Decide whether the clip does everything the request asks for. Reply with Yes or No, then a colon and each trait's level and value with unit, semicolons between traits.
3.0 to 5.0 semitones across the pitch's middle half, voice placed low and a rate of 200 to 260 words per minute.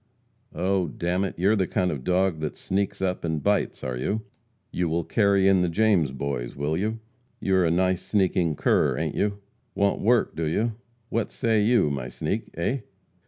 Yes: average, 4.0 semitones; very low, 95 Hz; fast, 205 wpm